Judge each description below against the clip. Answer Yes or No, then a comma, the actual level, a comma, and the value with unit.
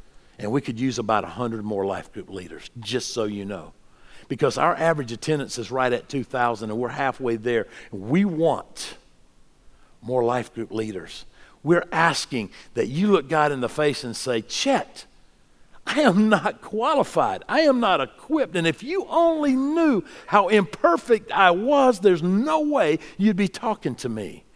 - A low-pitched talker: No, medium, 150 Hz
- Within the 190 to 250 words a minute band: No, average, 170 wpm